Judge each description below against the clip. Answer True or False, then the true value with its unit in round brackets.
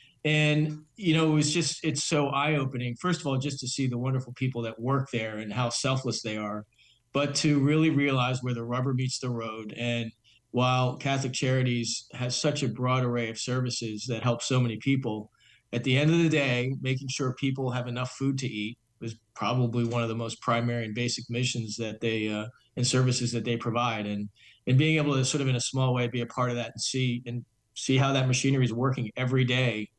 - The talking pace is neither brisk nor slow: False (220 wpm)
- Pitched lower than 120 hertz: False (125 Hz)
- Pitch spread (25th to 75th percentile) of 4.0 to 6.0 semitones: False (2.4 semitones)